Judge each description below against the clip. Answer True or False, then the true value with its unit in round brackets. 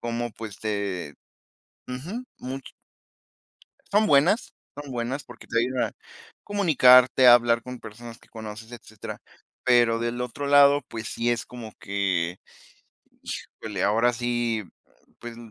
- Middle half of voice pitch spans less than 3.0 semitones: True (2.5 semitones)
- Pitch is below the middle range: True (120 Hz)